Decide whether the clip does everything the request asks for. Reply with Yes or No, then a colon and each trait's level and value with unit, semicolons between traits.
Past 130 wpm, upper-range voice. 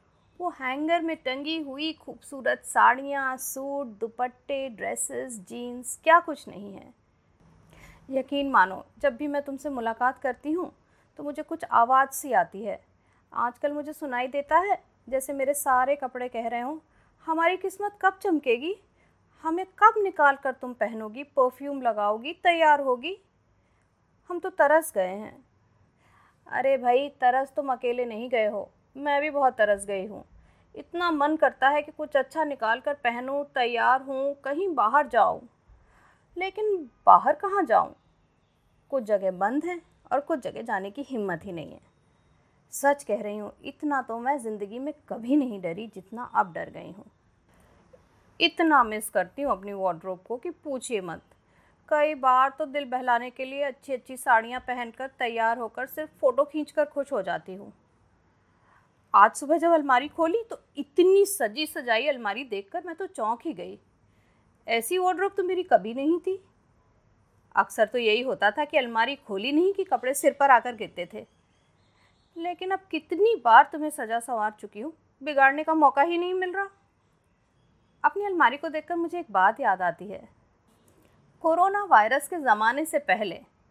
Yes: average, 165 wpm; very high, 280 Hz